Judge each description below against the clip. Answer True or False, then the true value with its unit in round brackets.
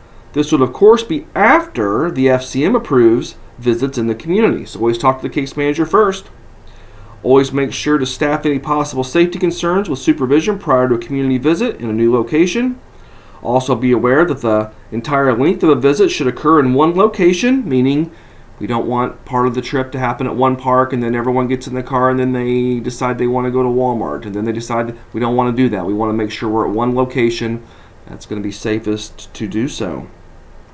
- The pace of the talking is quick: True (220 wpm)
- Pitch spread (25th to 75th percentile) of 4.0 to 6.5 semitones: False (3.3 semitones)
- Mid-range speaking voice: False (125 Hz)